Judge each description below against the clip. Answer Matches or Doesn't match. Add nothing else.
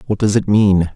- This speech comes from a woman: Doesn't match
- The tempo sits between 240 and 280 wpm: Matches